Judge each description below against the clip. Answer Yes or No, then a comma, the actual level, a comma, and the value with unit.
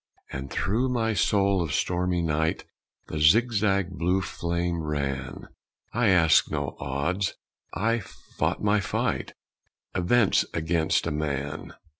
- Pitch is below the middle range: Yes, very low, 90 Hz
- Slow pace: Yes, slow, 120 wpm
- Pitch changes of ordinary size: Yes, average, 4.5 semitones